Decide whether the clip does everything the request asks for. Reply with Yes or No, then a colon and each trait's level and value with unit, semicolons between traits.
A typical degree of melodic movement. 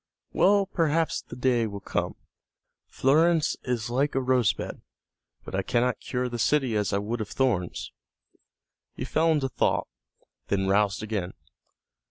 No: wide, 5.8 semitones